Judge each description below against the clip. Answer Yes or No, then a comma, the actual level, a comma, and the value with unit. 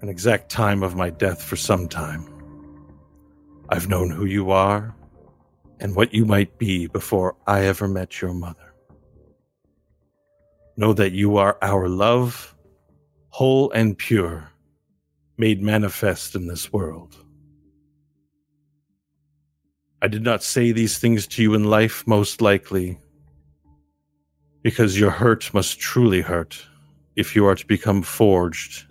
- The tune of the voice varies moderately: No, wide, 6.3 semitones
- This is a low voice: Yes, very low, 95 Hz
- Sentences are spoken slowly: Yes, slow, 130 wpm